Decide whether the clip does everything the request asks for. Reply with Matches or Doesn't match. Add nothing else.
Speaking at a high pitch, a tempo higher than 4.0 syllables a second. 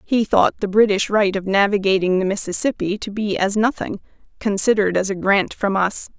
Matches